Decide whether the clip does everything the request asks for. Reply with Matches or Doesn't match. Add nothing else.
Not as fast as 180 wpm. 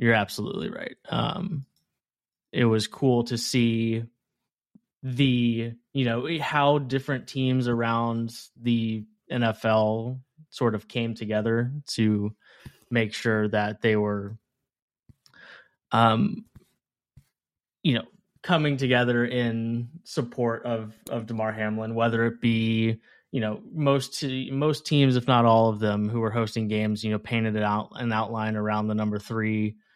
Matches